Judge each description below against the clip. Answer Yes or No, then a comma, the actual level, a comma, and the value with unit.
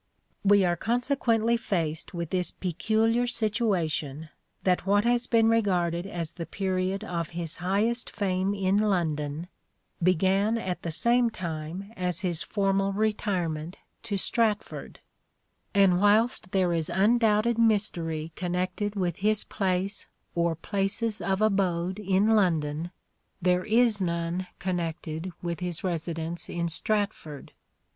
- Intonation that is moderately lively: Yes, average, 3.7 semitones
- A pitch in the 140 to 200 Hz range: Yes, high, 190 Hz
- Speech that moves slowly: Yes, slow, 130 wpm